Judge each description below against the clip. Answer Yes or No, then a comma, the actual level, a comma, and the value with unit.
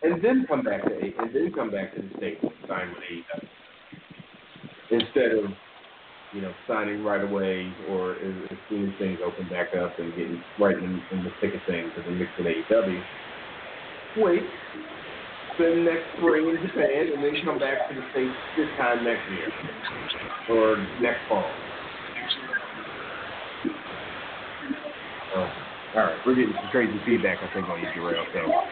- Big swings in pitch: Yes, wide, 6.2 semitones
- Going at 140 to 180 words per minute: Yes, average, 165 wpm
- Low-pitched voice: Yes, low, 105 Hz